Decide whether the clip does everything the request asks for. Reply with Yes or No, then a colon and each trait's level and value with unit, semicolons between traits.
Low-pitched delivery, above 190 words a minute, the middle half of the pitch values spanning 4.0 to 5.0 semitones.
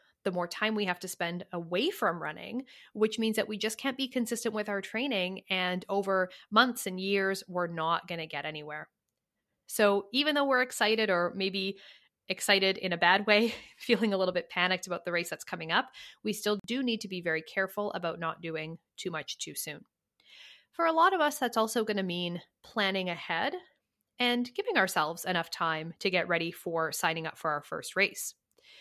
No: high, 195 Hz; average, 200 wpm; average, 4.3 semitones